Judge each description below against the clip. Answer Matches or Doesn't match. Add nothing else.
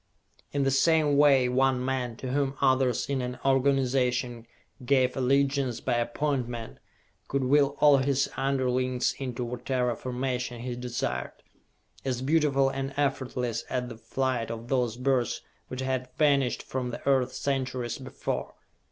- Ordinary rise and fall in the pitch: Doesn't match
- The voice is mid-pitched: Doesn't match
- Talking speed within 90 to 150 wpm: Matches